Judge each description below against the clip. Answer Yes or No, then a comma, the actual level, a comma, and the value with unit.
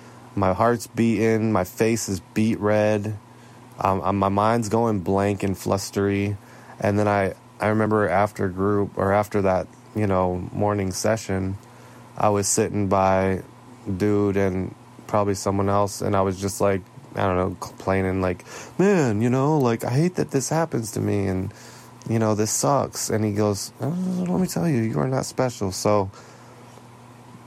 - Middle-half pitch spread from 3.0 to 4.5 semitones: Yes, average, 3.6 semitones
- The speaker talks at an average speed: Yes, average, 170 wpm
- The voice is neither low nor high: No, low, 105 Hz